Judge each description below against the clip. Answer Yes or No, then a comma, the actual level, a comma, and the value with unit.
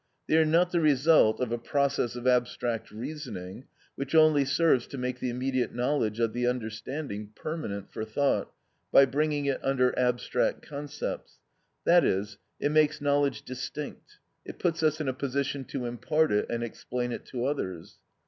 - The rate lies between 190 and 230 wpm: No, average, 165 wpm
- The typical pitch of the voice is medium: No, low, 130 Hz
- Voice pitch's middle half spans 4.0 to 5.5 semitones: No, average, 3.6 semitones